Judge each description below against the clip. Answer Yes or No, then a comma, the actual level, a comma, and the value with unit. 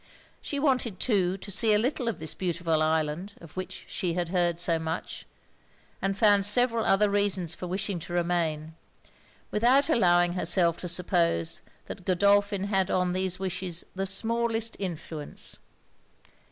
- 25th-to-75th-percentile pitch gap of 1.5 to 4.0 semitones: Yes, average, 2.9 semitones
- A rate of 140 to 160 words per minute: Yes, average, 150 wpm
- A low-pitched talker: No, medium, 185 Hz